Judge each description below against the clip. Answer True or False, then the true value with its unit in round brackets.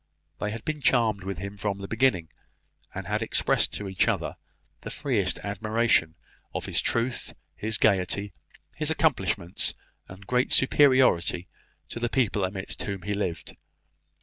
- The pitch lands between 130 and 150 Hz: False (105 Hz)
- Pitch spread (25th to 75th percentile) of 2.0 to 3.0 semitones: False (3.9 semitones)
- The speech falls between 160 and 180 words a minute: False (150 wpm)